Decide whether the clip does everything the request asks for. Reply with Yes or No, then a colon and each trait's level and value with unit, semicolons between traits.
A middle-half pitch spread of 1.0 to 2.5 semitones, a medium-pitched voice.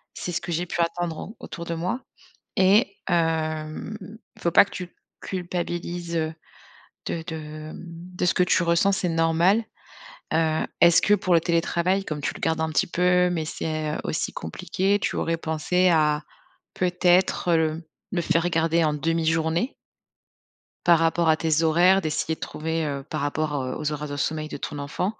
Yes: narrow, 2.1 semitones; medium, 165 Hz